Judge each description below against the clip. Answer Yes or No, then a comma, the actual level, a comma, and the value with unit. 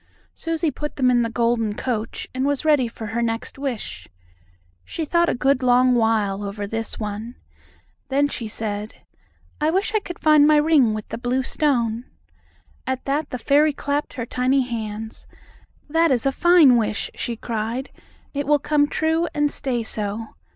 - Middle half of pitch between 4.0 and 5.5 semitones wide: Yes, average, 4.5 semitones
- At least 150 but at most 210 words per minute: Yes, average, 170 wpm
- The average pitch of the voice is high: Yes, very high, 255 Hz